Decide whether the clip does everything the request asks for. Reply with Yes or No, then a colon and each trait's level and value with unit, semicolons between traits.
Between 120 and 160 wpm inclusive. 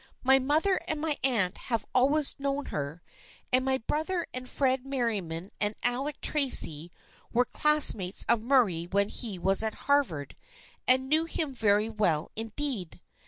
Yes: average, 150 wpm